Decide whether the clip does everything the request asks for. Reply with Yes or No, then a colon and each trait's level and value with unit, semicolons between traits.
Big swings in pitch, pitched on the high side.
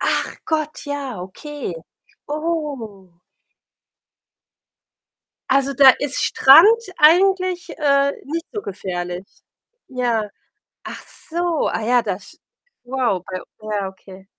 Yes: wide, 7.5 semitones; very high, 270 Hz